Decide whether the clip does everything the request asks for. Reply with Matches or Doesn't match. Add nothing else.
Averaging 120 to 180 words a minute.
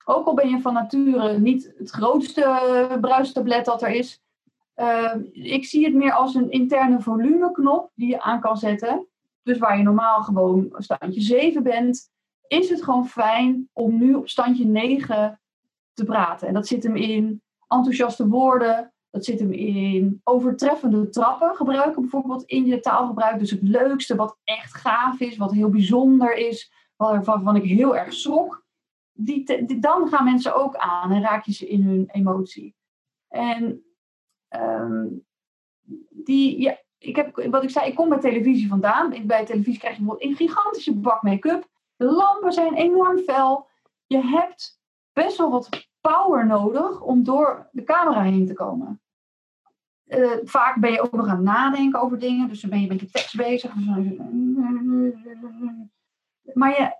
Matches